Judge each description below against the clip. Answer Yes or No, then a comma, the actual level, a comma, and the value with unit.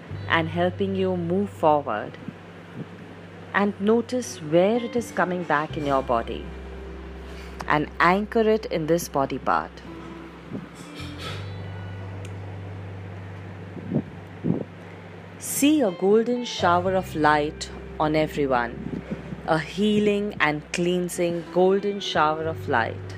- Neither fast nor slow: No, slow, 100 wpm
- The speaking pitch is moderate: Yes, medium, 150 Hz